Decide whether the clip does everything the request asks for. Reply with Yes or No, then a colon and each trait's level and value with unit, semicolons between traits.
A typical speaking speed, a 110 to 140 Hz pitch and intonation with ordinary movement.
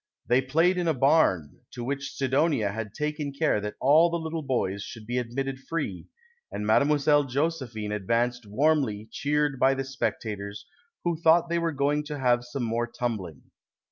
Yes: average, 175 wpm; low, 135 Hz; average, 4.6 semitones